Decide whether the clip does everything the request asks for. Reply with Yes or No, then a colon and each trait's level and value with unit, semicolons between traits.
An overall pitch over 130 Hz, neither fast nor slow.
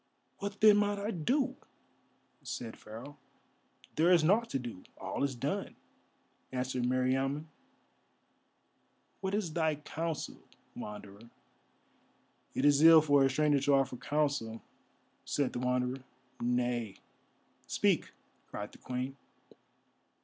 No: medium, 140 Hz; slow, 115 wpm